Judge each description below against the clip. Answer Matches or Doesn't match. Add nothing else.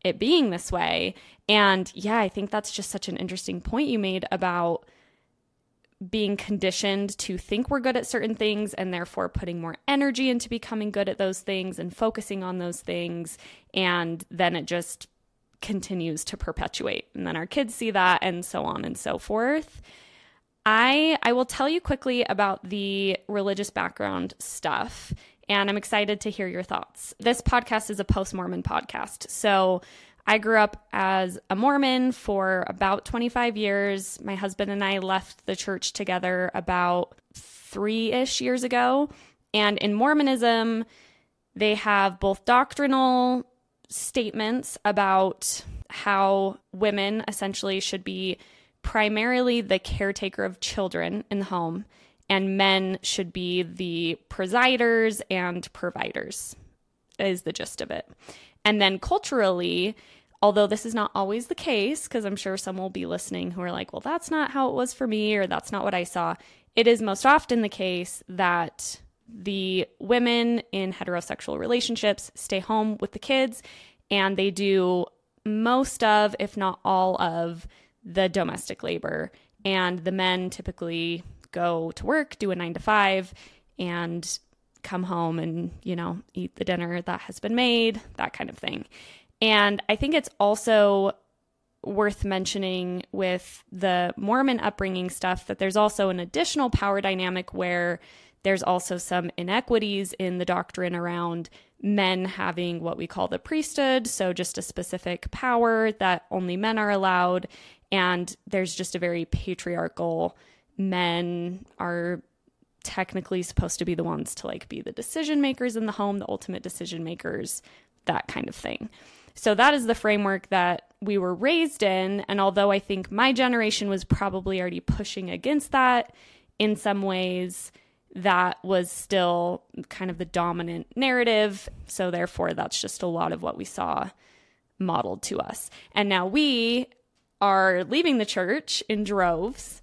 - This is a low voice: Doesn't match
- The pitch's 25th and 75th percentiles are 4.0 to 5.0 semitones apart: Doesn't match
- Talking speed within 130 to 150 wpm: Doesn't match